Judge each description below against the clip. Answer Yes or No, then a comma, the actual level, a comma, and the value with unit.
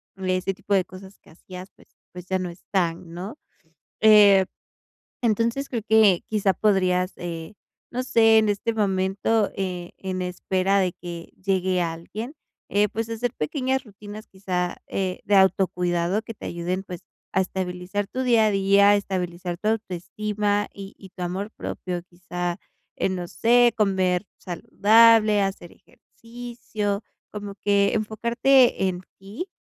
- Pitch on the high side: Yes, high, 195 Hz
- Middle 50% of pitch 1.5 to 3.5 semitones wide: Yes, average, 2.9 semitones